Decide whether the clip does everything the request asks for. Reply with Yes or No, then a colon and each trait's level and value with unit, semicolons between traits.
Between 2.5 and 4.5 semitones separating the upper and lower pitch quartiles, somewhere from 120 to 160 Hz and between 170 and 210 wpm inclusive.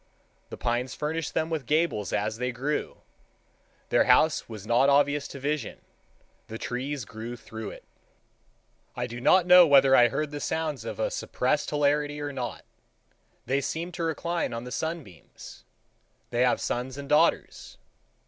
No: average, 4.0 semitones; medium, 140 Hz; average, 160 wpm